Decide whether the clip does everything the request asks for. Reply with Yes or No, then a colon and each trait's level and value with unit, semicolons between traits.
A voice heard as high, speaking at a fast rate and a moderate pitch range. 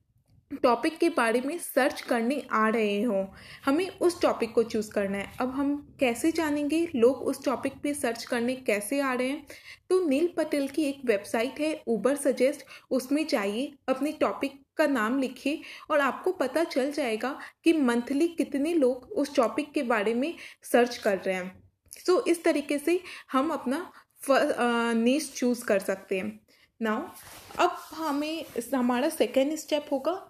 No: very high, 275 Hz; average, 165 wpm; average, 4.1 semitones